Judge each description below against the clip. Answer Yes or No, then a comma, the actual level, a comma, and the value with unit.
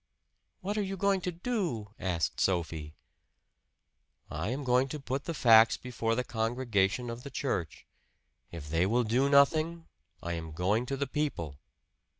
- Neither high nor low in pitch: No, low, 120 Hz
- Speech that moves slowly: No, average, 155 wpm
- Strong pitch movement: Yes, wide, 6.9 semitones